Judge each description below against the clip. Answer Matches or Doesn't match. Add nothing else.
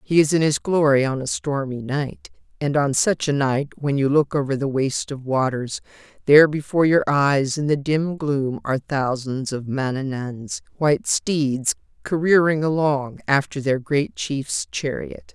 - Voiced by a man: Doesn't match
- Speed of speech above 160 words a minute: Matches